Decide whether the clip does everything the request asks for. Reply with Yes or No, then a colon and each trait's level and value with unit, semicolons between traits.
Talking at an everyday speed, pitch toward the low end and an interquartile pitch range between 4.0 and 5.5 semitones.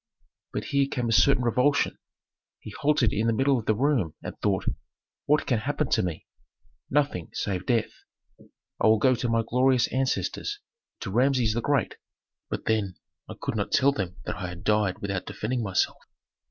Yes: average, 175 wpm; low, 115 Hz; average, 4.3 semitones